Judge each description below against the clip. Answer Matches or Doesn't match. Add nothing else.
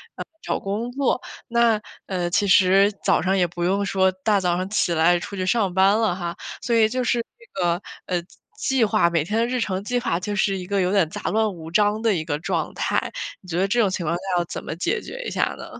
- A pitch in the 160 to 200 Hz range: Matches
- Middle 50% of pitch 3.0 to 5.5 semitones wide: Matches